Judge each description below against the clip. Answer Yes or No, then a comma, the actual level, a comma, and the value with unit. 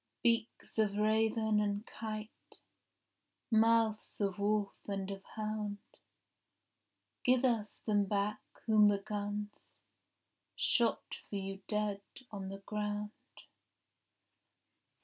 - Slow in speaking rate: Yes, slow, 100 wpm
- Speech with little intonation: Yes, narrow, 1.3 semitones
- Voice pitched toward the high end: Yes, high, 210 Hz